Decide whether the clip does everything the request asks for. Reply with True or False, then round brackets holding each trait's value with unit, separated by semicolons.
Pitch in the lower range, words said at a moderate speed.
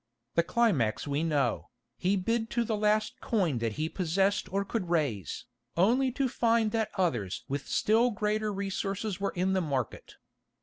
False (195 Hz; 165 wpm)